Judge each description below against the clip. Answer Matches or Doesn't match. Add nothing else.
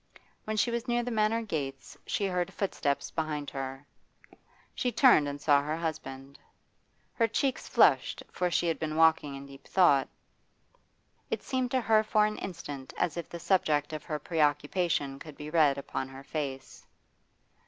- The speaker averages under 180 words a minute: Matches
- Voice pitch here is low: Doesn't match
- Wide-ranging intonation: Matches